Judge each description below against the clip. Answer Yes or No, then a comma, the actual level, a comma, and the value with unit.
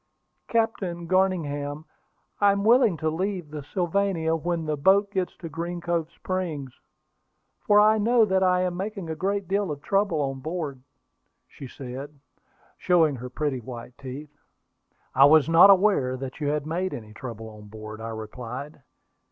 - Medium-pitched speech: Yes, medium, 160 Hz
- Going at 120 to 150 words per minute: No, average, 160 wpm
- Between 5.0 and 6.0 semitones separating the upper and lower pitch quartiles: Yes, wide, 5.5 semitones